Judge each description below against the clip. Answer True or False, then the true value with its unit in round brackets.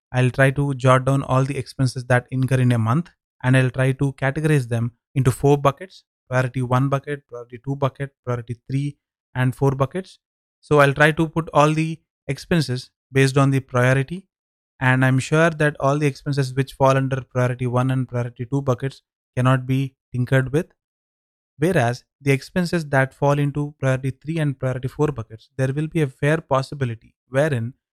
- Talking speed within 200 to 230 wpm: False (180 wpm)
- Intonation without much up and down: True (2.1 semitones)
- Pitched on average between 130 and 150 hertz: True (135 Hz)